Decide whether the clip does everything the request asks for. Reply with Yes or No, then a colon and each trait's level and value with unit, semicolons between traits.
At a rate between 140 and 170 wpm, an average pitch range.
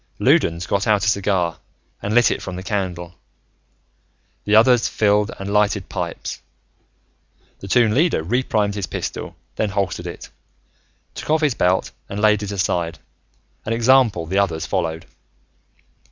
Yes: average, 145 wpm; average, 3.4 semitones